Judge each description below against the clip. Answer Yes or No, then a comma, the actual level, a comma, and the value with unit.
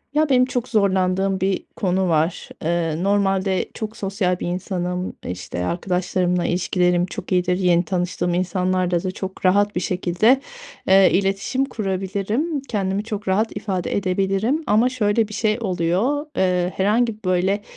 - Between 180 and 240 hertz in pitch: Yes, high, 190 Hz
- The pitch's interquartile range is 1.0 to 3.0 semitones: Yes, narrow, 2.6 semitones